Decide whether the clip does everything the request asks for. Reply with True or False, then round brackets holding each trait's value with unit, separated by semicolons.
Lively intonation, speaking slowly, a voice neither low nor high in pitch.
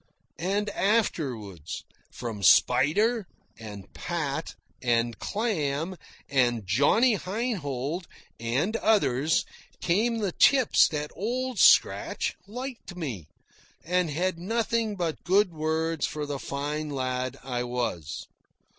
True (8.1 semitones; 105 wpm; 160 Hz)